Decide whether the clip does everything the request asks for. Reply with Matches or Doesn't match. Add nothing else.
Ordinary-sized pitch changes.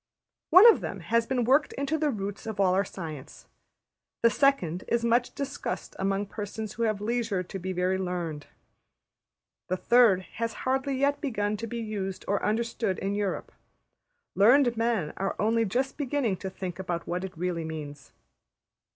Matches